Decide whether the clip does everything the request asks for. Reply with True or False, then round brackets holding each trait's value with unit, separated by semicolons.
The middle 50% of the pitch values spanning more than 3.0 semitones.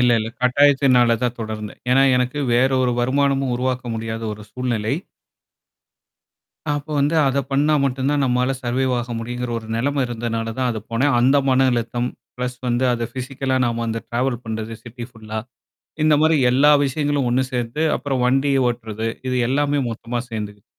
False (2.6 semitones)